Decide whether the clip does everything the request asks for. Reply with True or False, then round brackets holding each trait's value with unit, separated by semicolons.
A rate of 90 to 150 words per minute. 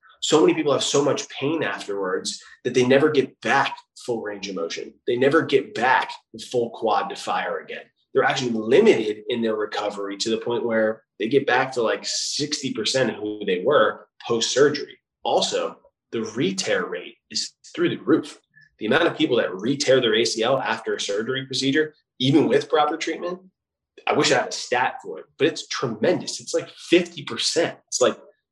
False (185 wpm)